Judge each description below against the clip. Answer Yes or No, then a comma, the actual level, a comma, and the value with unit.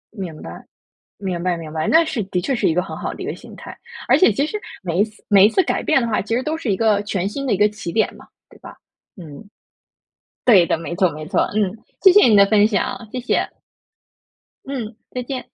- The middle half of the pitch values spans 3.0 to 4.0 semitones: No, average, 5.2 semitones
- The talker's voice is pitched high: Yes, high, 210 Hz